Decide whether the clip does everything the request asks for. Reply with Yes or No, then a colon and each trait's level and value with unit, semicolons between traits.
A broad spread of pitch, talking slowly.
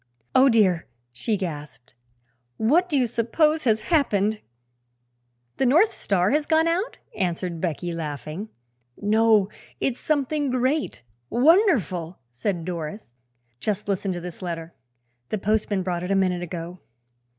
Yes: wide, 6.8 semitones; slow, 130 wpm